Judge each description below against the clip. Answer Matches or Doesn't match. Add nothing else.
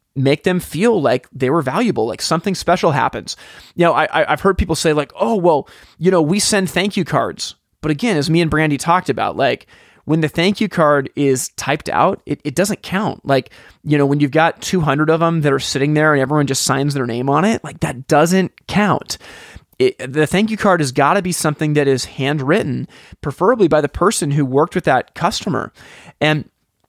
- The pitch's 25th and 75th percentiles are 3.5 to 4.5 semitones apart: Matches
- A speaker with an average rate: Doesn't match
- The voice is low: Doesn't match